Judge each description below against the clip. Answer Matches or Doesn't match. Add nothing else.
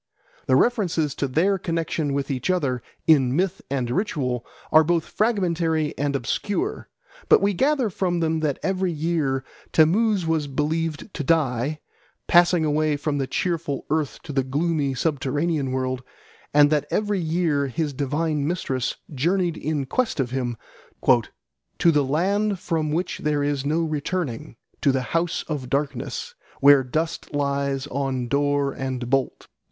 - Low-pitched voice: Doesn't match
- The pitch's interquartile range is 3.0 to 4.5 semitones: Matches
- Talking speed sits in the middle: Matches